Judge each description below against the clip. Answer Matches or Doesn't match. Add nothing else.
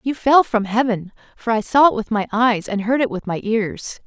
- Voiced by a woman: Matches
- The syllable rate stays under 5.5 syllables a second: Matches